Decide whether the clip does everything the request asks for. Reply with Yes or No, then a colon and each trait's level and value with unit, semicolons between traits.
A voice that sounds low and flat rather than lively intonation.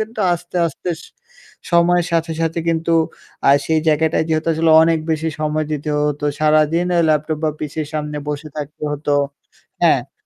No: medium, 155 Hz; narrow, 1.5 semitones